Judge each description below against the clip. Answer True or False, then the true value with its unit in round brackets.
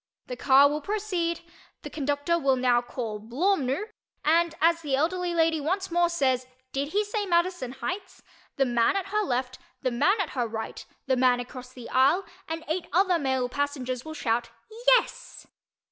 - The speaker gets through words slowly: False (175 wpm)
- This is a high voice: True (290 Hz)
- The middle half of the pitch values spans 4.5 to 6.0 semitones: True (5.5 semitones)